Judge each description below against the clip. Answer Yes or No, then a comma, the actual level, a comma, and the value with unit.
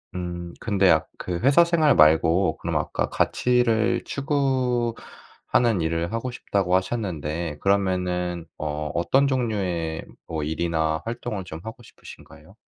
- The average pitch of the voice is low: Yes, very low, 95 Hz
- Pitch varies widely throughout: Yes, wide, 6.4 semitones